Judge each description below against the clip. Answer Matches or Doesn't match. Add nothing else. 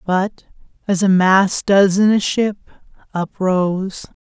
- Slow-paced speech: Matches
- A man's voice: Doesn't match